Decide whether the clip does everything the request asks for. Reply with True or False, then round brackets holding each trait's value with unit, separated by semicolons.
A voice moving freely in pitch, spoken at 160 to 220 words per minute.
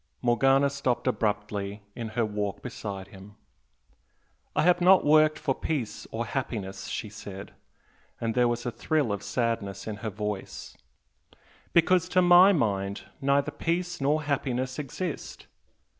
False (6.1 semitones; 140 wpm)